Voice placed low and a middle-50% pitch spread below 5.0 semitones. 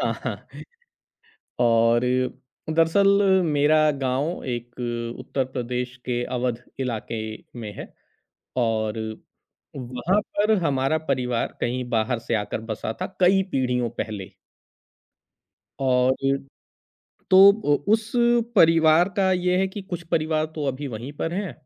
No: low, 130 Hz; wide, 5.4 semitones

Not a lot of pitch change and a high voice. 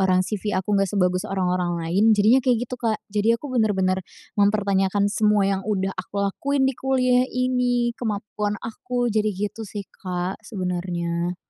No: average, 3.6 semitones; high, 205 Hz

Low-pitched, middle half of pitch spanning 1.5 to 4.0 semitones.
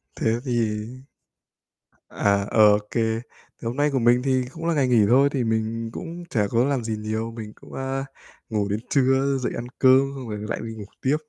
Yes: low, 120 Hz; average, 3.3 semitones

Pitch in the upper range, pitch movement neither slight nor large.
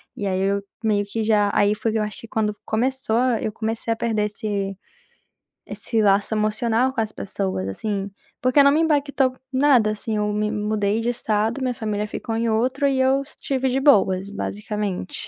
Yes: high, 220 Hz; average, 3.3 semitones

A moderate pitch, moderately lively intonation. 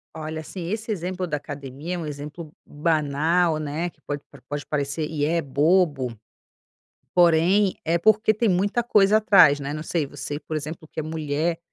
Yes: medium, 160 Hz; average, 3.5 semitones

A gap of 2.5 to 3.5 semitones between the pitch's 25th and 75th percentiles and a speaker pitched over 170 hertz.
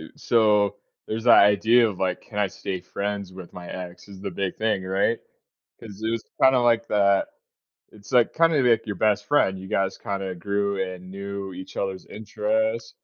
No: average, 2.9 semitones; low, 100 Hz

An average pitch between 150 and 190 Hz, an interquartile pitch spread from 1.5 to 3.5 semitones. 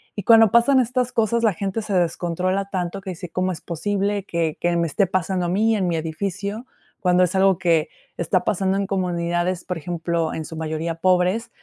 Yes: medium, 185 Hz; average, 2.8 semitones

